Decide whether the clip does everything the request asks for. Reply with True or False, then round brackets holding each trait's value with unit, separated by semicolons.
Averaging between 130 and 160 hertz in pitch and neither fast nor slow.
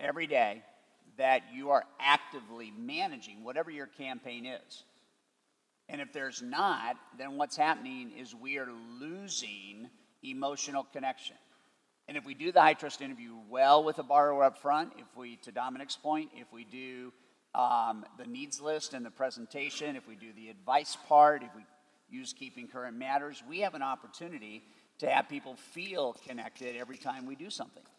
True (140 Hz; 170 wpm)